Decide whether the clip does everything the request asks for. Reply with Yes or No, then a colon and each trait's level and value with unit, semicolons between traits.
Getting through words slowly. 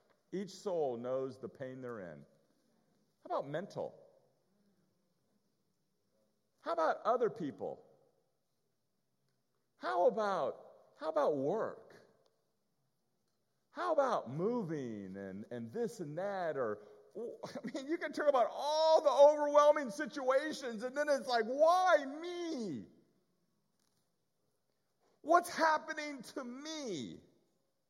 Yes: slow, 105 wpm